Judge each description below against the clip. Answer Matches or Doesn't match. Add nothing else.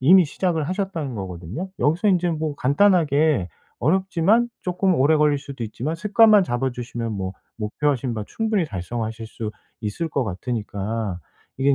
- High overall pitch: Doesn't match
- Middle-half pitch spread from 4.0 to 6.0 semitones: Doesn't match